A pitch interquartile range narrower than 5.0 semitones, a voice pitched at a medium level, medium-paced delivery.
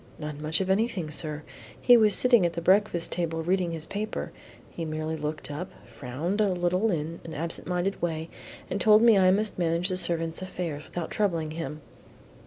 Yes: average, 3.3 semitones; medium, 170 Hz; average, 190 wpm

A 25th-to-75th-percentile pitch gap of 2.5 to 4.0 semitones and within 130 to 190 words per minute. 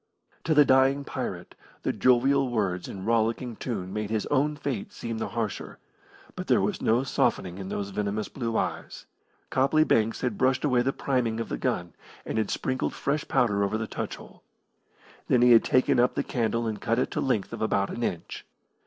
No: average, 3.4 semitones; average, 200 wpm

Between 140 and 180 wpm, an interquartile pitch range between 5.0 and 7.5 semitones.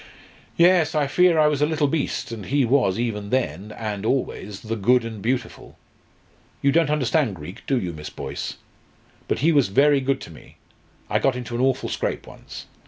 No: average, 190 wpm; wide, 5.4 semitones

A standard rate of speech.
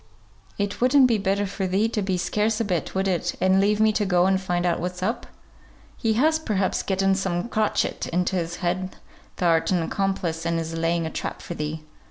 No: fast, 210 wpm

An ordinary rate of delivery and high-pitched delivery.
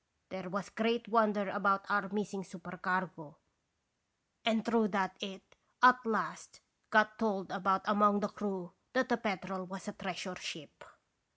Yes: average, 145 wpm; high, 200 Hz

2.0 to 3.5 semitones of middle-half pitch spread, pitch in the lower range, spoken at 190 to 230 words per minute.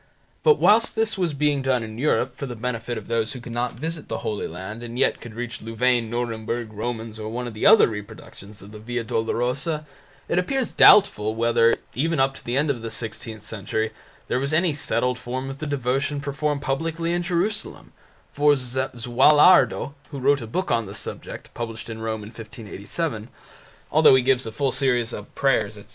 No: average, 4.2 semitones; low, 125 Hz; average, 195 wpm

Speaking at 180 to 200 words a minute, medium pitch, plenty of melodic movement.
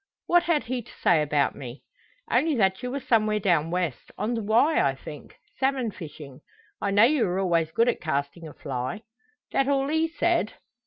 No: average, 195 wpm; high, 210 Hz; wide, 8.8 semitones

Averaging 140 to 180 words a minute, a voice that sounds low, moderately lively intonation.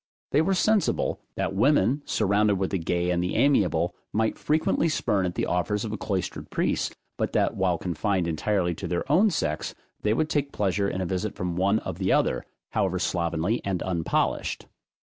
No: average, 190 wpm; very low, 95 Hz; average, 3.9 semitones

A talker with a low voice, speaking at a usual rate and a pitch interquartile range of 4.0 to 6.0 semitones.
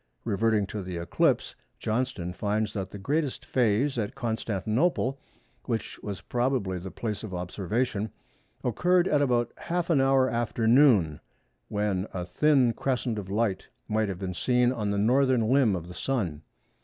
Yes: low, 110 Hz; average, 155 wpm; average, 4.7 semitones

